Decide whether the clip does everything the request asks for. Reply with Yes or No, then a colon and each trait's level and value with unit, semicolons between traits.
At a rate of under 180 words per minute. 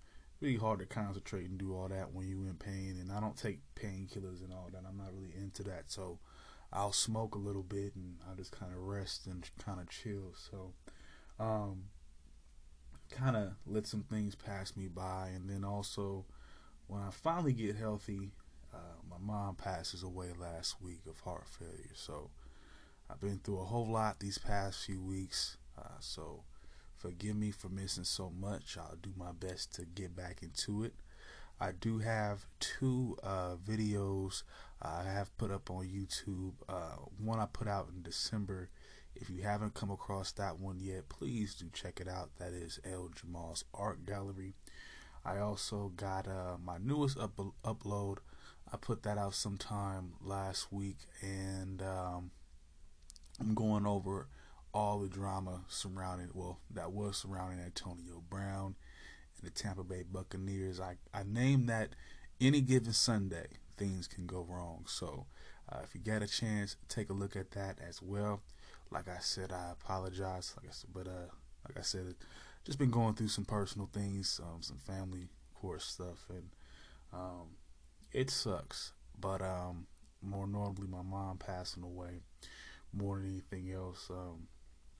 Yes: average, 165 wpm